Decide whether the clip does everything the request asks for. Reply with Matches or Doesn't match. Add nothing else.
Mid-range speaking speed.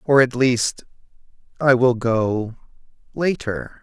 Doesn't match